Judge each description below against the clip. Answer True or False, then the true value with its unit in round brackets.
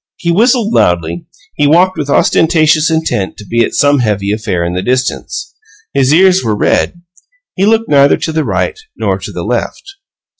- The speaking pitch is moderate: True (145 Hz)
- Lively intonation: True (8.7 semitones)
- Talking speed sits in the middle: True (180 wpm)